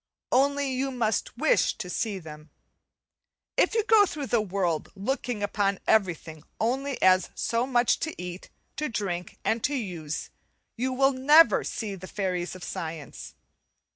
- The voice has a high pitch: Yes, high, 215 Hz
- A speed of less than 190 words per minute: Yes, average, 150 wpm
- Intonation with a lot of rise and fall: Yes, wide, 6.6 semitones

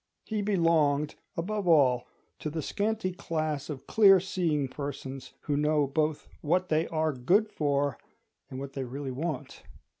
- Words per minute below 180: Yes, average, 150 wpm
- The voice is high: No, medium, 155 Hz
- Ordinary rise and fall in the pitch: Yes, average, 4.0 semitones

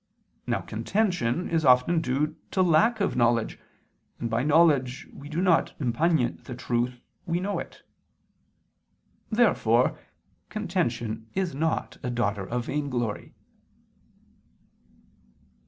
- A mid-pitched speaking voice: Yes, medium, 145 Hz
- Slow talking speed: Yes, slow, 110 wpm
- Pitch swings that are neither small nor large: No, wide, 6.1 semitones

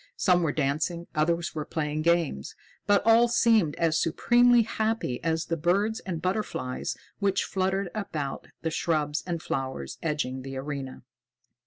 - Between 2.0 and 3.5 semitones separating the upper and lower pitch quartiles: No, average, 4.9 semitones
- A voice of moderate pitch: Yes, medium, 165 Hz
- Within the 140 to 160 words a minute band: Yes, average, 145 wpm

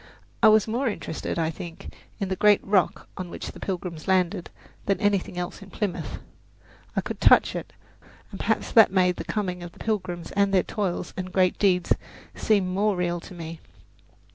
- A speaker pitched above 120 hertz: Yes, medium, 185 Hz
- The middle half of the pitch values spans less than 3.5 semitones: Yes, narrow, 2.5 semitones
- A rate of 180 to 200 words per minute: Yes, average, 190 wpm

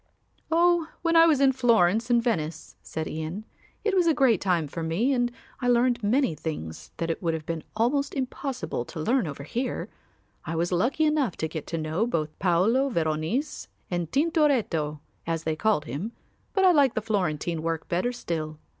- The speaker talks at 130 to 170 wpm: No, average, 185 wpm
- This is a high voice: Yes, high, 210 Hz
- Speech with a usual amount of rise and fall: No, wide, 8.6 semitones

